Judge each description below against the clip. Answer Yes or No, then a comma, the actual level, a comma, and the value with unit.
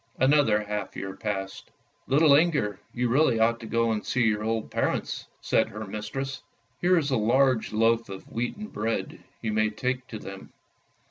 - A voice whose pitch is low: Yes, low, 115 Hz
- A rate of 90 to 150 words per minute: No, average, 185 wpm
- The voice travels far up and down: No, average, 3.6 semitones